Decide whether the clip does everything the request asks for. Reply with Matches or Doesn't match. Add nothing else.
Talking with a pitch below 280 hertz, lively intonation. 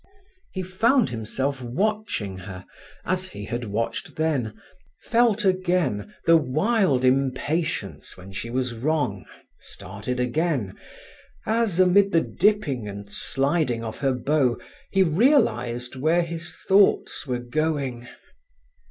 Matches